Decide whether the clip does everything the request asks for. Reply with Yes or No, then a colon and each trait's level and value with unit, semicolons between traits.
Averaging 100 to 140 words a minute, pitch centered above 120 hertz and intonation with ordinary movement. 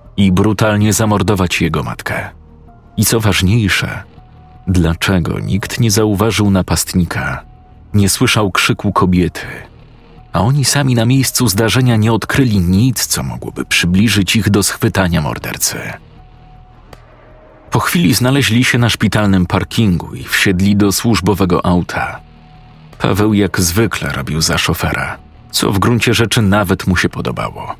No: average, 125 wpm; low, 100 Hz; average, 3.7 semitones